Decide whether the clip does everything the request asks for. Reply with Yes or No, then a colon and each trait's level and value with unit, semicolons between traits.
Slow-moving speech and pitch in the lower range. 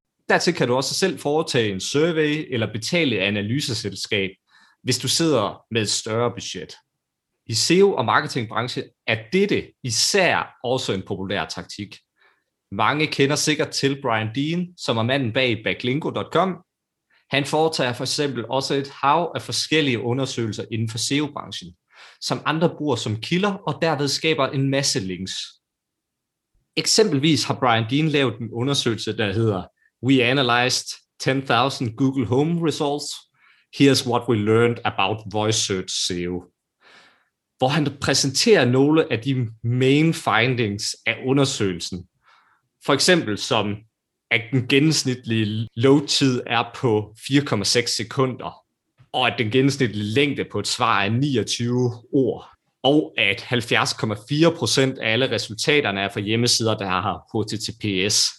Yes: slow, 135 wpm; low, 125 Hz